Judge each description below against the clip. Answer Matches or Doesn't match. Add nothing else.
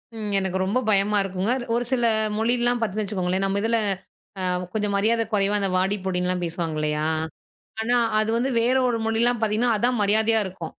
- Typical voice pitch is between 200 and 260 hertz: Matches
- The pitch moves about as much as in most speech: Matches